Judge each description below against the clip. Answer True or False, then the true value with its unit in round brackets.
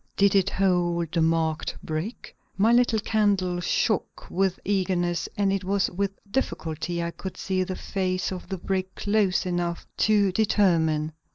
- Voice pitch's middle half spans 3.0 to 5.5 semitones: False (2.4 semitones)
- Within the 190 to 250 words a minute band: False (155 wpm)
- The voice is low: False (185 Hz)